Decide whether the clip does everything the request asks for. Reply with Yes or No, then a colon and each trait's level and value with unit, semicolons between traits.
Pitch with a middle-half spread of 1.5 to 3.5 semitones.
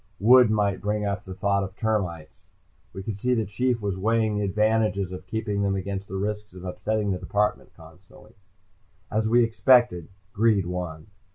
Yes: narrow, 2.4 semitones